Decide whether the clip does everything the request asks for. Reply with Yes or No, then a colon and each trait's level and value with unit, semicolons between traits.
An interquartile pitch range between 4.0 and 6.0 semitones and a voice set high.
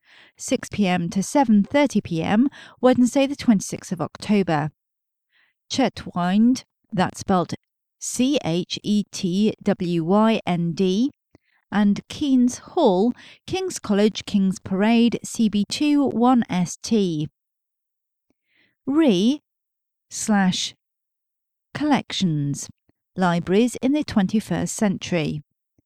Yes: average, 5.2 semitones; high, 205 Hz